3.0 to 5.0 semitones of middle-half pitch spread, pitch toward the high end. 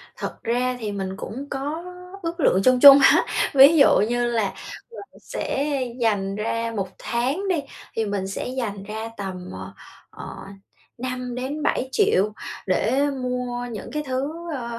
Yes: average, 4.5 semitones; high, 245 Hz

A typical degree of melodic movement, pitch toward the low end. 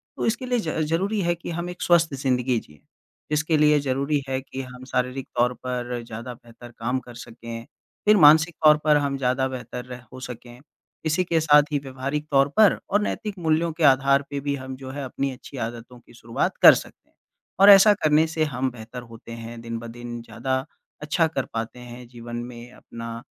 Yes: average, 4.2 semitones; low, 130 Hz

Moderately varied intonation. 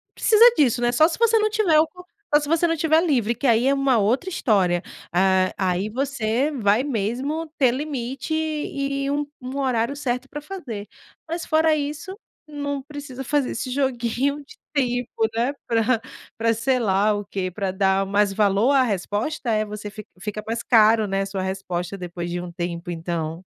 No: wide, 6.0 semitones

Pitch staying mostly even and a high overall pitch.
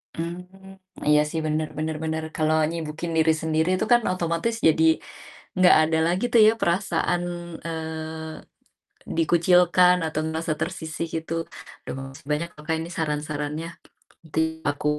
No: narrow, 1.9 semitones; medium, 160 Hz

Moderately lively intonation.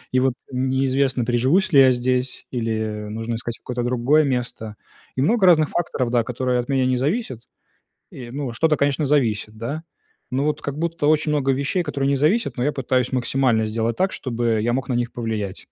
Yes: average, 3.2 semitones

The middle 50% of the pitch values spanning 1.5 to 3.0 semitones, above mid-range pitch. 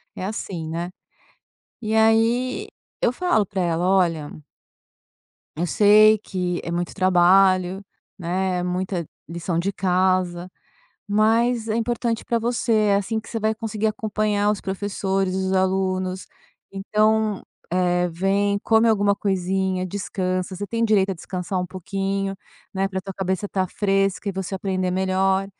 Yes: narrow, 2.5 semitones; high, 195 Hz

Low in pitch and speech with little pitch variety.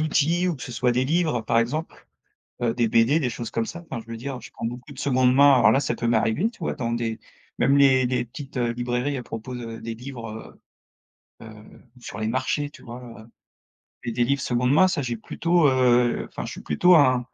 No: low, 125 Hz; average, 3.2 semitones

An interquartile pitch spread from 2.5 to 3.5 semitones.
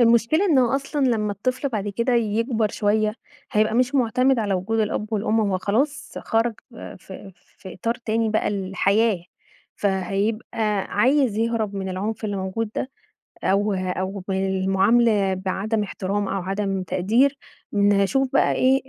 Yes: average, 3.1 semitones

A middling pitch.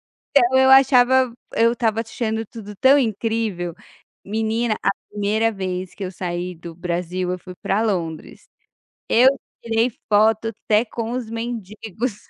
No: high, 220 Hz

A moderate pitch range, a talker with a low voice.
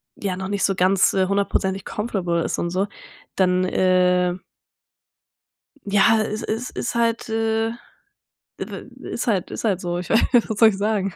No: average, 3.1 semitones; high, 195 Hz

